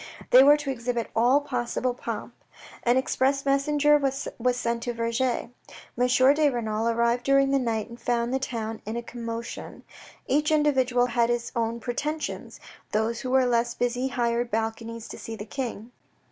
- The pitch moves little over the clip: Yes, narrow, 2.3 semitones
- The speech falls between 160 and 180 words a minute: Yes, average, 165 wpm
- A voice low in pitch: No, high, 245 Hz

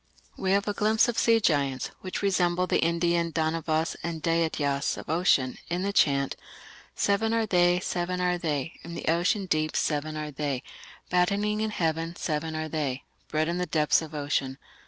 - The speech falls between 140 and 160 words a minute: No, average, 180 wpm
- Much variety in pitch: No, average, 3.0 semitones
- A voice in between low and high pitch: Yes, medium, 165 Hz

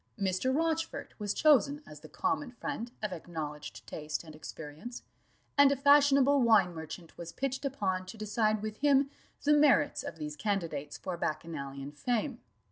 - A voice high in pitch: Yes, high, 210 Hz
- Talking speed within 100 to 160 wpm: Yes, average, 155 wpm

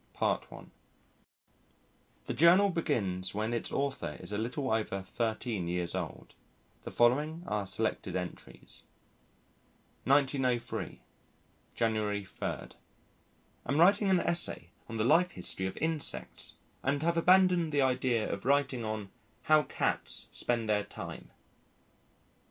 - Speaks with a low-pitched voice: Yes, low, 120 Hz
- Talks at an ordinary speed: No, slow, 125 wpm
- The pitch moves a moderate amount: No, wide, 6.6 semitones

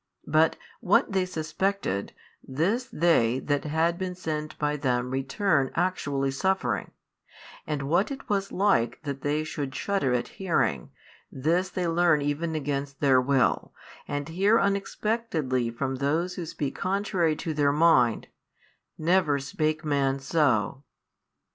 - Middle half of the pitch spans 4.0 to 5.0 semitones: Yes, average, 4.7 semitones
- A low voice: No, medium, 155 Hz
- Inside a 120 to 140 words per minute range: Yes, slow, 135 wpm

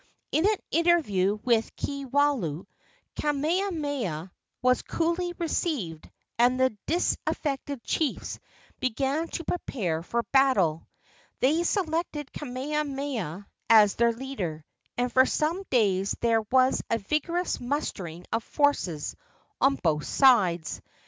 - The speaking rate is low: Yes, slow, 110 wpm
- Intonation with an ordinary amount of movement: No, wide, 6.8 semitones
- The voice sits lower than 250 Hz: No, very high, 260 Hz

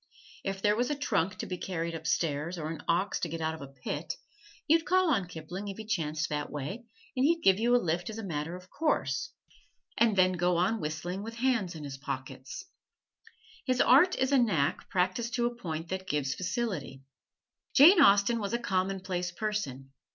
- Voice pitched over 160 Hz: Yes, medium, 185 Hz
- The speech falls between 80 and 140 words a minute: No, average, 195 wpm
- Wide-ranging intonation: Yes, wide, 6.4 semitones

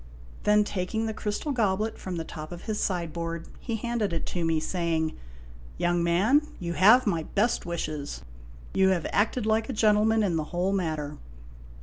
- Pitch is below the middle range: No, medium, 185 Hz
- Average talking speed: Yes, average, 180 wpm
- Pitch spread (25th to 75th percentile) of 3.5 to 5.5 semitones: Yes, average, 4.4 semitones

